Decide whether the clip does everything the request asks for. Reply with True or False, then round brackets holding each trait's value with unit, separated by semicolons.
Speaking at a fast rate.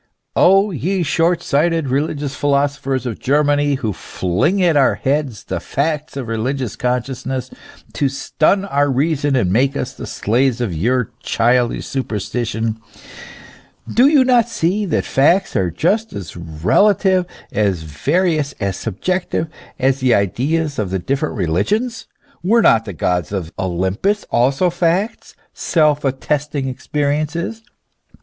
False (135 wpm)